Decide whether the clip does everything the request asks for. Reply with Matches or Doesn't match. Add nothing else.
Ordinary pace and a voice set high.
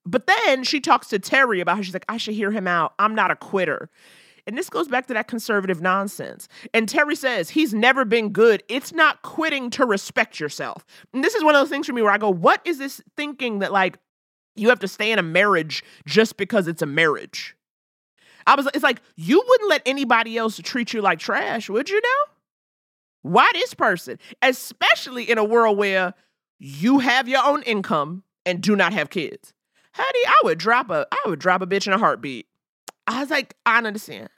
Doesn't match